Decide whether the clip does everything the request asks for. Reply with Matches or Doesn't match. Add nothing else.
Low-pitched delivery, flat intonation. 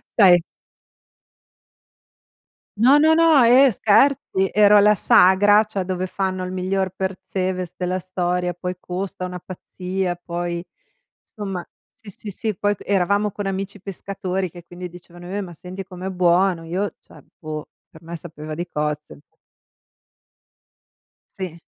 Doesn't match